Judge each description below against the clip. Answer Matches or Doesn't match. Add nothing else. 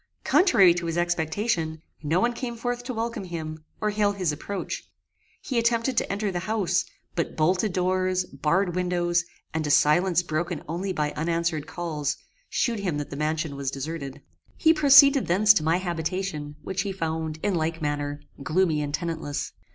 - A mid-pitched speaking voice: Matches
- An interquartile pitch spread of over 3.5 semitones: Matches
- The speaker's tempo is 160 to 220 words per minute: Matches